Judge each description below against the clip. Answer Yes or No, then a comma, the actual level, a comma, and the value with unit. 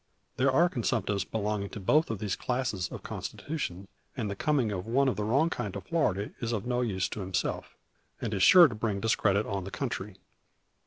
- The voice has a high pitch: No, low, 110 Hz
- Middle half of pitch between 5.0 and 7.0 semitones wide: No, average, 4.6 semitones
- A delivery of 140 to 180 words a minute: No, average, 200 wpm